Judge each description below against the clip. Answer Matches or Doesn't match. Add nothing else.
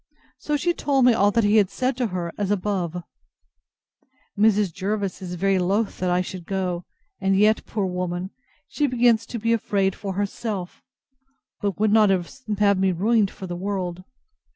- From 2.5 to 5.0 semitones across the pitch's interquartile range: Matches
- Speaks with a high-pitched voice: Matches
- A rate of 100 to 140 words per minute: Doesn't match